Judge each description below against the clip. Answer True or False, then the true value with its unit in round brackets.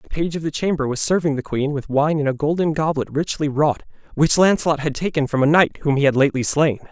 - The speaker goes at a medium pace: False (250 wpm)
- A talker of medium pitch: True (150 Hz)